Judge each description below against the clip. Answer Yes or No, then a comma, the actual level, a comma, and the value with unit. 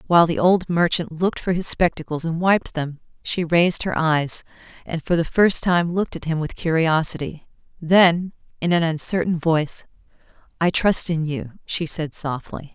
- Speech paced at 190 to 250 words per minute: No, average, 175 wpm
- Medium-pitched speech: Yes, medium, 165 Hz